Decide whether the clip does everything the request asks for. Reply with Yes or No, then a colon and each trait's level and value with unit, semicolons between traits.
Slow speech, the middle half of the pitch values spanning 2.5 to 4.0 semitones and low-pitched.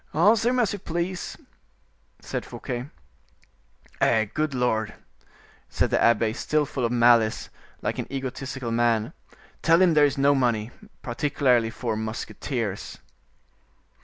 No: slow, 130 wpm; average, 4.8 semitones; low, 125 Hz